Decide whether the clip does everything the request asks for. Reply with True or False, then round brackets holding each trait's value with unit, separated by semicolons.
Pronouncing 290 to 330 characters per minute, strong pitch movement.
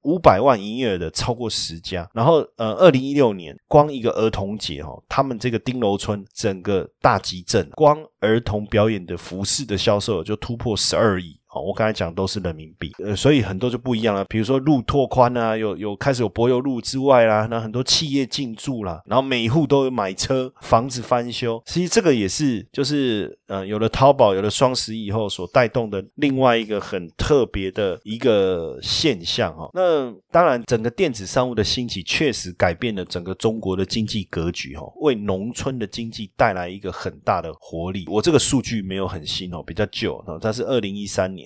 False (310 characters per minute; 4.7 semitones)